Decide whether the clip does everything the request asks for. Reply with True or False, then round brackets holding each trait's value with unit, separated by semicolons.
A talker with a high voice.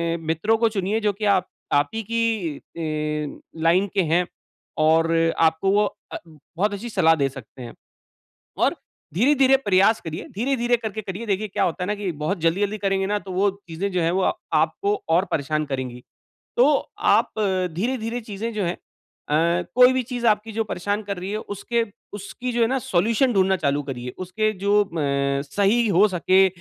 True (195 Hz)